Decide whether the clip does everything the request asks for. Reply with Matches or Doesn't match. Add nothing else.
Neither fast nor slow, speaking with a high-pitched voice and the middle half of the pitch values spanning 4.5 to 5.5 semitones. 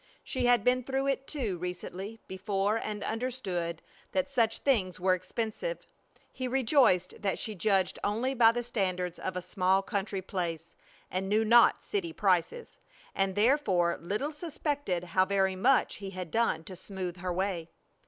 Matches